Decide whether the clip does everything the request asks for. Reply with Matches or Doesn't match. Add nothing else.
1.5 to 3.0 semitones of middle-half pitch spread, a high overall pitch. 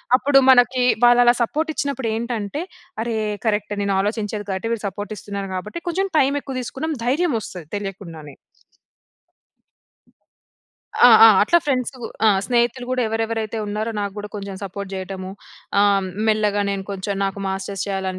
Doesn't match